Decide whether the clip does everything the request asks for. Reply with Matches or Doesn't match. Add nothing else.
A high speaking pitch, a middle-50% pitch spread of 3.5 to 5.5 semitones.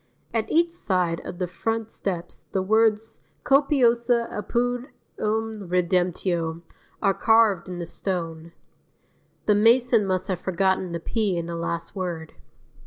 Matches